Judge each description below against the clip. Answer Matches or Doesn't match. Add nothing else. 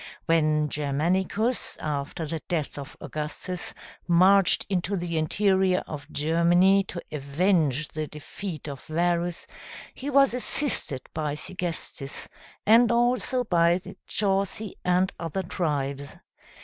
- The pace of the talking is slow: Matches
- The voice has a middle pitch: Matches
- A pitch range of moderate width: Matches